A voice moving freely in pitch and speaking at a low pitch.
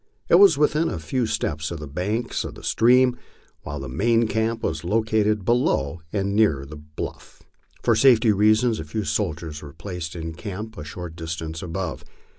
Yes: wide, 5.9 semitones; very low, 95 Hz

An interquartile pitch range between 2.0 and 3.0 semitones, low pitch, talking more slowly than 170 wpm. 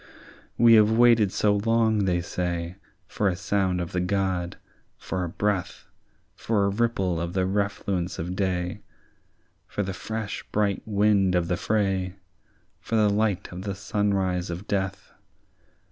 Yes: narrow, 2.5 semitones; very low, 95 Hz; average, 150 wpm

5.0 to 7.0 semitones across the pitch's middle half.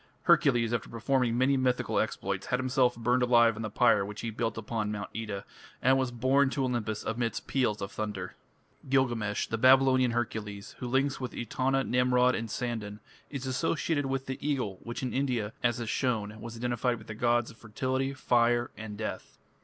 No: average, 2.8 semitones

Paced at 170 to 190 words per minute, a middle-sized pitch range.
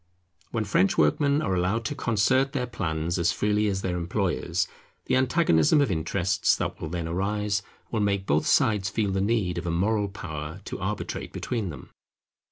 Yes: average, 175 wpm; average, 4.0 semitones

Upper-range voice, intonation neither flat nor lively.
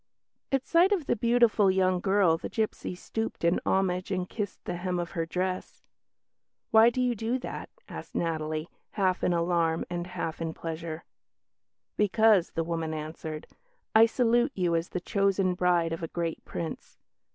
No: medium, 180 Hz; average, 4.6 semitones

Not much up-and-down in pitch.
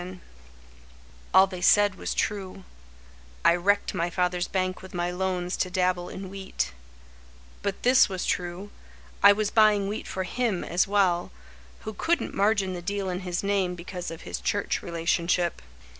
Yes: narrow, 2.2 semitones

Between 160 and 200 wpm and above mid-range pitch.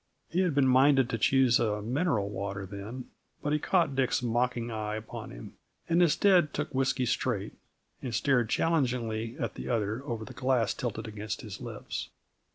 No: average, 170 wpm; low, 125 Hz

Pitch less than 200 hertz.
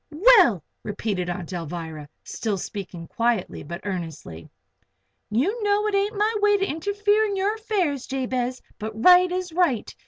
No: very high, 265 Hz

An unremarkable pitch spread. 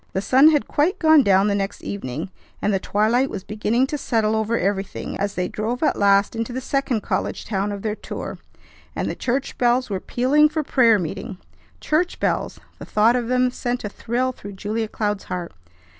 Yes: average, 4.1 semitones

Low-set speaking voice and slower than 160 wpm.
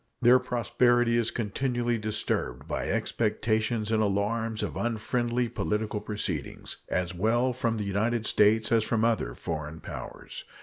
Yes: low, 110 Hz; slow, 135 wpm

